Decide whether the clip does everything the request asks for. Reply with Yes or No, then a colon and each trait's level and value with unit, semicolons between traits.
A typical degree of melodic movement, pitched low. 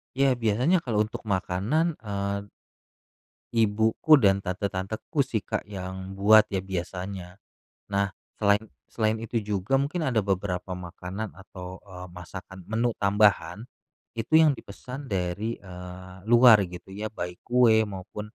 Yes: average, 3.3 semitones; low, 100 Hz